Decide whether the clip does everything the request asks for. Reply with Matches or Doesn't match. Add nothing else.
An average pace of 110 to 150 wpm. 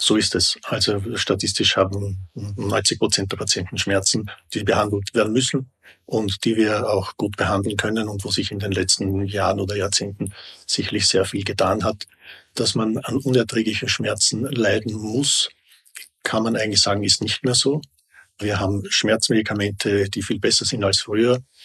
Doesn't match